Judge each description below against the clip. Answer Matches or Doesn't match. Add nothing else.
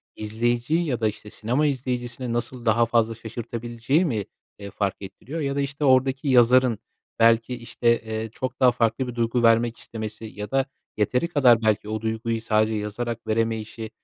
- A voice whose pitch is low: Matches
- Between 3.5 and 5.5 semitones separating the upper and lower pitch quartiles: Doesn't match